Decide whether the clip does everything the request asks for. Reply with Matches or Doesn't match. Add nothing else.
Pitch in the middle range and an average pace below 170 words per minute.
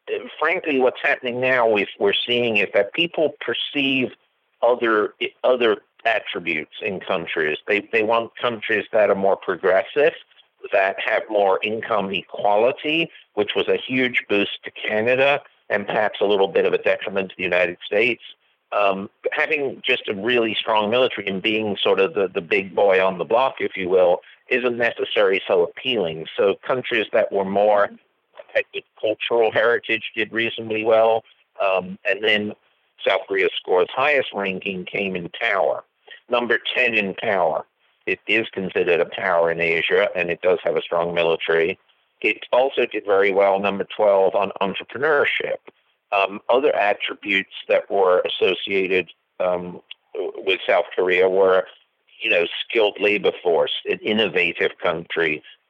Matches